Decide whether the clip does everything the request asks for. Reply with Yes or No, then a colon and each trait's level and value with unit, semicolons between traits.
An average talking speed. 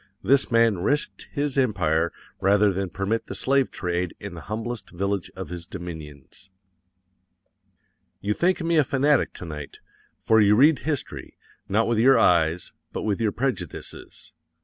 Yes: average, 150 wpm